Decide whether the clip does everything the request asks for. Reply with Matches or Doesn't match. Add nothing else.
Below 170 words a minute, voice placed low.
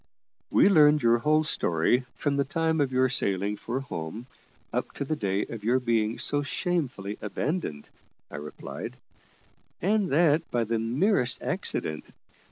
Matches